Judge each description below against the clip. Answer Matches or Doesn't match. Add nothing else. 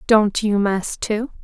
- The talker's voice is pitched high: Matches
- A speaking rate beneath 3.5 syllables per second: Matches